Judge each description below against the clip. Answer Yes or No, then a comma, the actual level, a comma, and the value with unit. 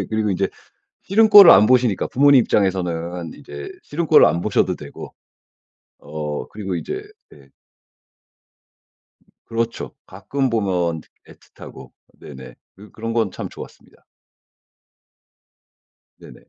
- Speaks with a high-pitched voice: No, low, 105 Hz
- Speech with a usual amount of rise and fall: No, wide, 7.3 semitones